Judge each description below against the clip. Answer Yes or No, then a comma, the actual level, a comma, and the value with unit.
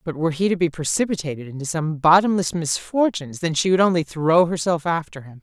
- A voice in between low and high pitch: Yes, medium, 165 Hz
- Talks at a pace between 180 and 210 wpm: Yes, average, 200 wpm